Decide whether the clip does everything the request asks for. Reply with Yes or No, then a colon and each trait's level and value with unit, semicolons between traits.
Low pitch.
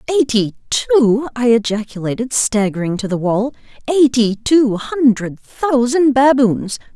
No: high, 240 Hz